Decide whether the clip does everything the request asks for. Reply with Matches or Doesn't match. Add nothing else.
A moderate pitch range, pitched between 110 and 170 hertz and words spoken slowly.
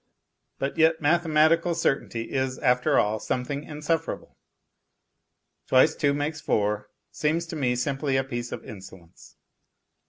Matches